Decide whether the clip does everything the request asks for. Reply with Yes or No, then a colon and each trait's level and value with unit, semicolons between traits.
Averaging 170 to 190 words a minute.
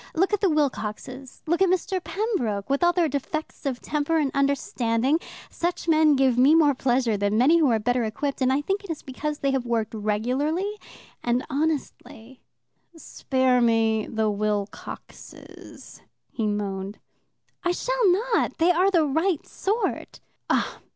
No: average, 155 wpm